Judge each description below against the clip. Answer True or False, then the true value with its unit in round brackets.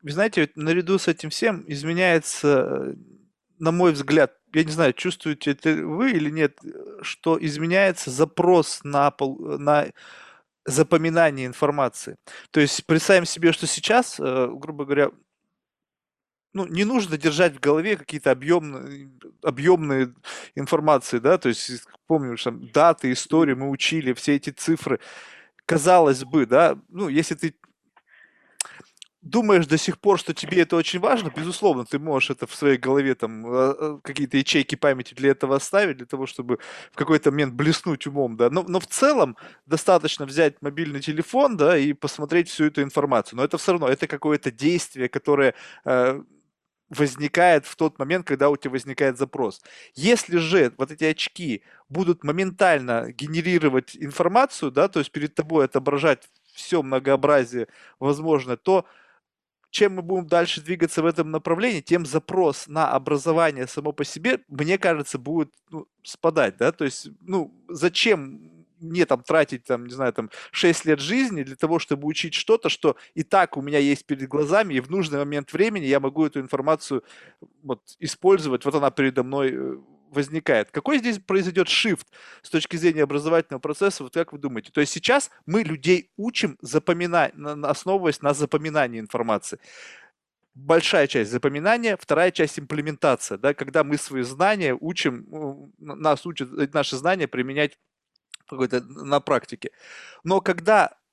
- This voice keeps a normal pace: True (150 wpm)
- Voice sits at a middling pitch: True (155 Hz)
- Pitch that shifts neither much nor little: True (3.8 semitones)